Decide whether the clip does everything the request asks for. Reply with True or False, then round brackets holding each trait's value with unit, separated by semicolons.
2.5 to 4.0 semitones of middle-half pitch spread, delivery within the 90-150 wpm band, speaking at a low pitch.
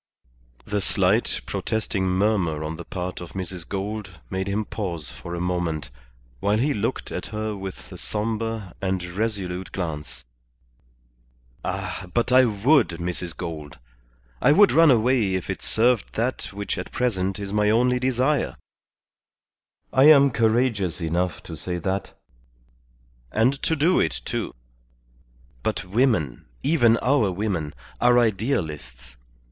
False (4.9 semitones; 135 wpm; 100 Hz)